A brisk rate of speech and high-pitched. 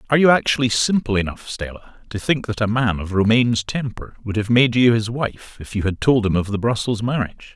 No: fast, 230 wpm; low, 115 Hz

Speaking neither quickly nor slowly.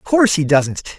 No: fast, 245 wpm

